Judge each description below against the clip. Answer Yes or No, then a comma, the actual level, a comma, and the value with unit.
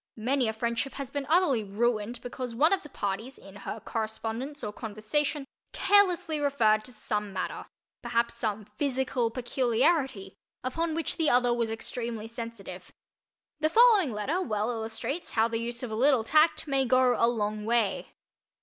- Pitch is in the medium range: No, high, 240 Hz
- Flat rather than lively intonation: No, average, 4.0 semitones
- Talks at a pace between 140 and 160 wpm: Yes, average, 155 wpm